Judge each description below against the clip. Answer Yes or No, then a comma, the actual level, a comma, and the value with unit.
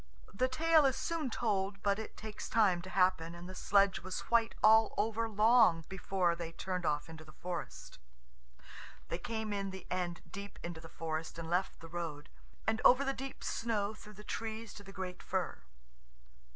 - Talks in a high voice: Yes, high, 195 Hz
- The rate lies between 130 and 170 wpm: No, average, 185 wpm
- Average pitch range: Yes, average, 4.2 semitones